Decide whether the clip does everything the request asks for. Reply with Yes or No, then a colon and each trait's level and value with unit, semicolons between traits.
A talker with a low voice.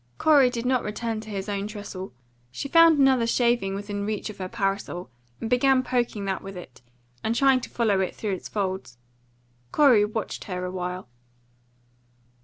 No: high, 210 Hz